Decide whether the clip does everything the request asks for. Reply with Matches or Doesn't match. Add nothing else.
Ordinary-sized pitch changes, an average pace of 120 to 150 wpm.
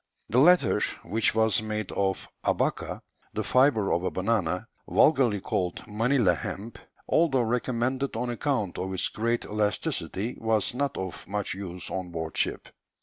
Matches